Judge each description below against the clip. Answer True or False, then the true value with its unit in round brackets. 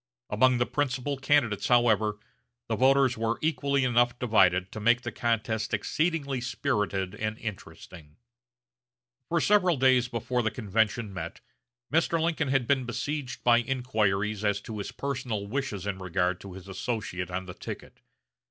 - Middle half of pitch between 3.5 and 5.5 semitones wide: True (4.4 semitones)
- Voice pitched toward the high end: False (120 Hz)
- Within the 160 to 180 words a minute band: False (150 wpm)